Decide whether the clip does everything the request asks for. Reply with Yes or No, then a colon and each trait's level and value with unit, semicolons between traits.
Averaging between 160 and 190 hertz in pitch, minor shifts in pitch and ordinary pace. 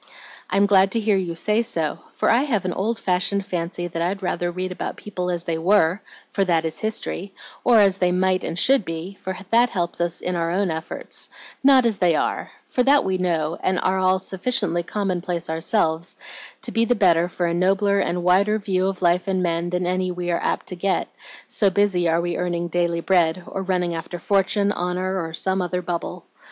No: medium, 185 Hz; narrow, 2.3 semitones; fast, 210 wpm